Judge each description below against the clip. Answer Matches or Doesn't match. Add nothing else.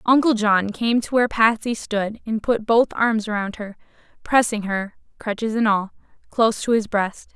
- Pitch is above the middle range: Matches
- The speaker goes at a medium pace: Matches